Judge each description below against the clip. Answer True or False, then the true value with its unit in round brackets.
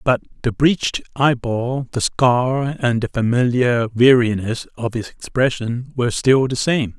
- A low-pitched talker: True (125 Hz)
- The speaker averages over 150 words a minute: False (145 wpm)